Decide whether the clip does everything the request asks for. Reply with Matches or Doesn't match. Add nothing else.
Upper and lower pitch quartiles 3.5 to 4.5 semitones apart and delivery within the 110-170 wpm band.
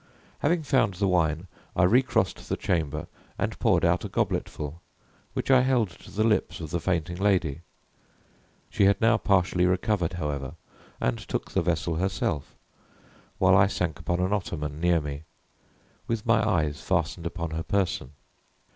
Matches